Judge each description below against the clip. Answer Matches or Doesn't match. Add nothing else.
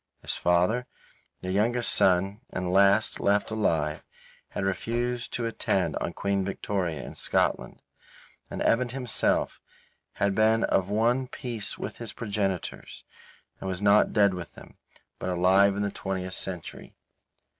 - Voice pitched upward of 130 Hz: Doesn't match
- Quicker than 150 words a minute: Doesn't match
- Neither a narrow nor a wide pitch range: Matches